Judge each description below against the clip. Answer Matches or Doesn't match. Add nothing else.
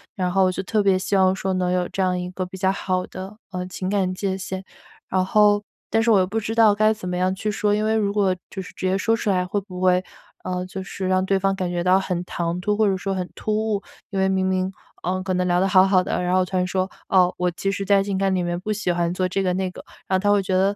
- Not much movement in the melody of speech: Matches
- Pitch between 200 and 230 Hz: Doesn't match